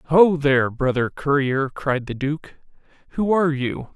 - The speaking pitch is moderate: Yes, medium, 145 Hz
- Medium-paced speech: Yes, average, 150 wpm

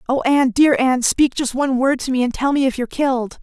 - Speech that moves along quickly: Yes, fast, 280 wpm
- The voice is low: No, very high, 260 Hz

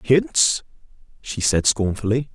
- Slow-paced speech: Yes, slow, 100 wpm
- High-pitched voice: No, low, 125 Hz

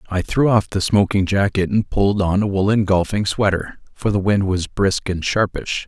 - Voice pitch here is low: Yes, low, 100 Hz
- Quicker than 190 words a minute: Yes, fast, 205 wpm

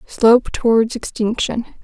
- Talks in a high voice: Yes, high, 230 Hz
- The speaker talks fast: No, slow, 100 wpm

